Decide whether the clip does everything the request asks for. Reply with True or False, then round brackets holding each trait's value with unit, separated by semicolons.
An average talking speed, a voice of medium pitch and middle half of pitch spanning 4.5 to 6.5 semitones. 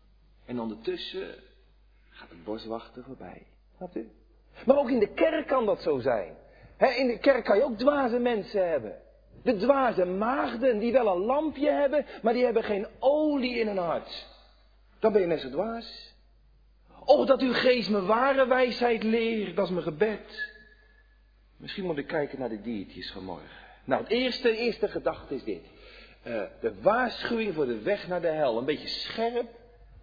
False (170 wpm; 235 Hz; 5.1 semitones)